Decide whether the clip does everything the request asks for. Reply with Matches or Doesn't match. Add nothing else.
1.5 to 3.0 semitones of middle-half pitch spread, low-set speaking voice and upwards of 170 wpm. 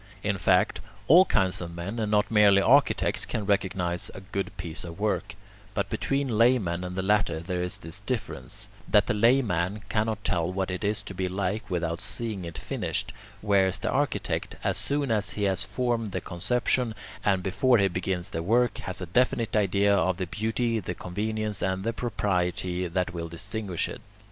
Doesn't match